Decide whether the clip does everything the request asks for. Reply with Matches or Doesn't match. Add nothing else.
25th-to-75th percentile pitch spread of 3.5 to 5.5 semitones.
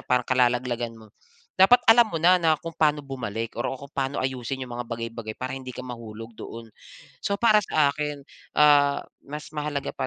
Matches